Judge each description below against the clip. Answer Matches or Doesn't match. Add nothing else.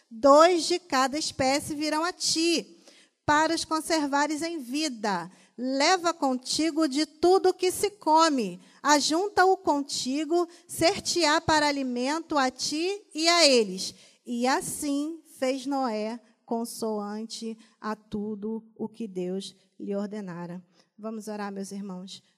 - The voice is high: Matches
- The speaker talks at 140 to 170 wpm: Doesn't match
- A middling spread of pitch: Doesn't match